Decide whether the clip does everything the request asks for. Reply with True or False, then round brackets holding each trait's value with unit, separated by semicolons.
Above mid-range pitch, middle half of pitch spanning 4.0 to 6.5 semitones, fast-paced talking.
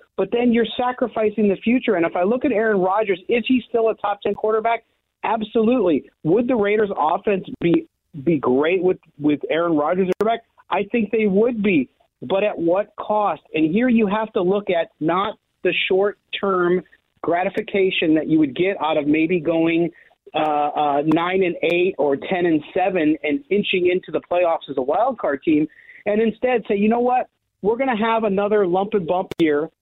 False (195 Hz; 5.0 semitones; 190 wpm)